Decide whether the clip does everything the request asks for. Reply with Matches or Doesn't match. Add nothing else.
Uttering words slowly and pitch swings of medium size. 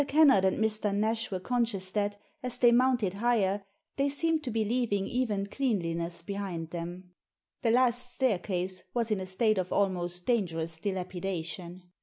Doesn't match